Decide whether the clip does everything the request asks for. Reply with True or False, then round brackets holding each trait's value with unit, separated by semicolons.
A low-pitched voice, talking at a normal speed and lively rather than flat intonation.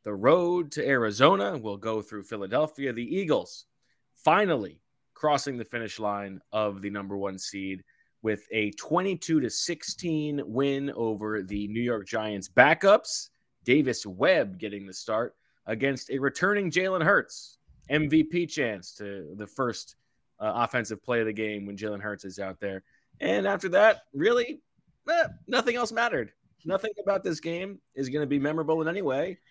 True (130 Hz; 160 wpm; 8.7 semitones)